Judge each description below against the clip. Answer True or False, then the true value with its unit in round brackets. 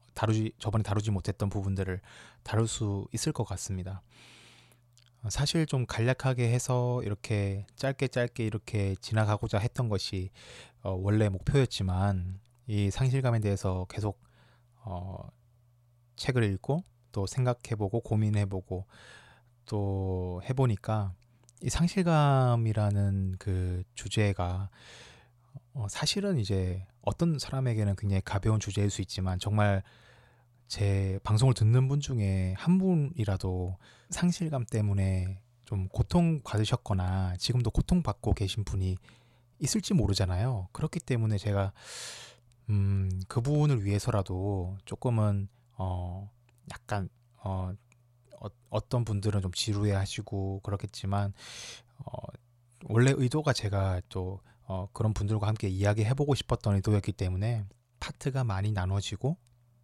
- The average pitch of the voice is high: False (110 Hz)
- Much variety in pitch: False (3.8 semitones)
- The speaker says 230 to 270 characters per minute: True (265 characters per minute)